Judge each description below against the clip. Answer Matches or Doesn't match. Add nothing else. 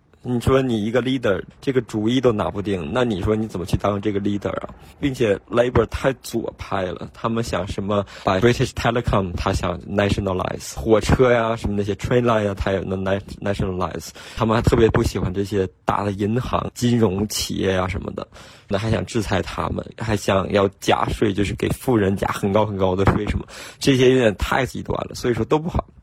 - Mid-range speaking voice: Doesn't match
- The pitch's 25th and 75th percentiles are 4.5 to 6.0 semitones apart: Doesn't match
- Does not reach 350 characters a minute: Doesn't match